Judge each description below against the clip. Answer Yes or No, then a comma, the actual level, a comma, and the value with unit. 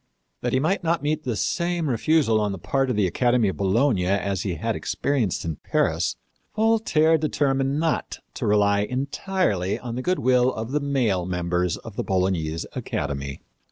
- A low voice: Yes, low, 120 Hz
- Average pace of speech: Yes, average, 175 wpm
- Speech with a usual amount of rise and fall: No, wide, 7.3 semitones